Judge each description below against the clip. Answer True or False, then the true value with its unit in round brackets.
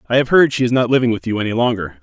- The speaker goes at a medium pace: False (325 wpm)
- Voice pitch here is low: True (115 Hz)